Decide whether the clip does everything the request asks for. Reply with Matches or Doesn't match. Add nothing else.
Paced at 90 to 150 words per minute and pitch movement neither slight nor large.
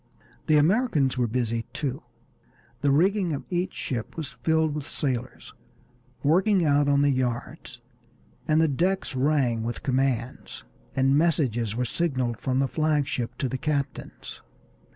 Matches